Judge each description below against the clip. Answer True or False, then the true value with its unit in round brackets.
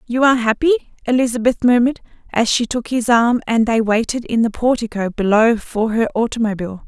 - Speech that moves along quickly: False (175 wpm)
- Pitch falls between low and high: False (235 Hz)